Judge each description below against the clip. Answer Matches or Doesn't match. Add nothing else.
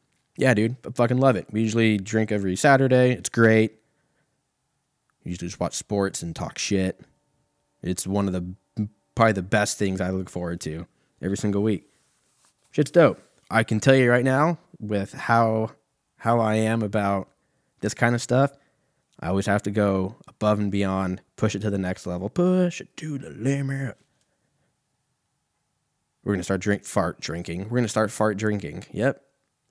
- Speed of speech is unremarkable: Matches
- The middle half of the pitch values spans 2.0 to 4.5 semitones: Doesn't match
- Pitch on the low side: Matches